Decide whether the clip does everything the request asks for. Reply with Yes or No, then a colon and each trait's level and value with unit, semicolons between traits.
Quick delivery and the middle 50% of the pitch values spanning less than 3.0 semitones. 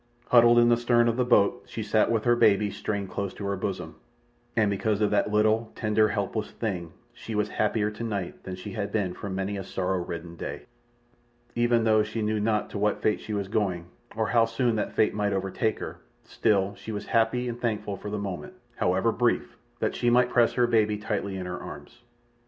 Yes: fast, 210 wpm; narrow, 2.5 semitones